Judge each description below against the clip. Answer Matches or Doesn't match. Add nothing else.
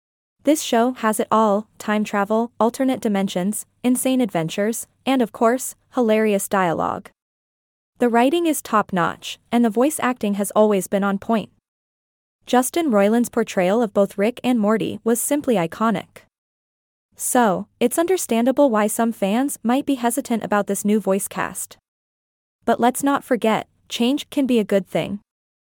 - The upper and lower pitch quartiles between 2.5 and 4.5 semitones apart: Matches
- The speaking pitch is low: Doesn't match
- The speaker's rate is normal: Matches